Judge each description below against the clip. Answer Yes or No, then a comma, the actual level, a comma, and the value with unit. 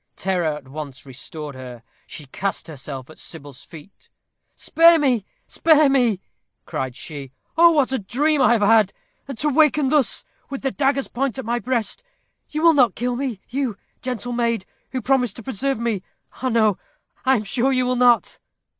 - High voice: Yes, high, 240 Hz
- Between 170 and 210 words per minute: Yes, average, 175 wpm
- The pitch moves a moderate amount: No, wide, 6.9 semitones